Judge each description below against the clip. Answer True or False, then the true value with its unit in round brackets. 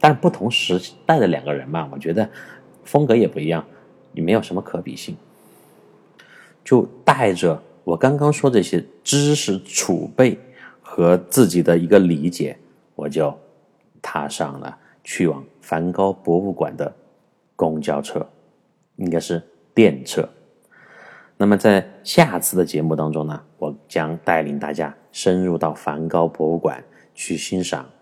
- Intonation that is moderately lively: True (3.5 semitones)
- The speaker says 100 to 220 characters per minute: True (210 characters per minute)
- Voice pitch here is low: True (85 Hz)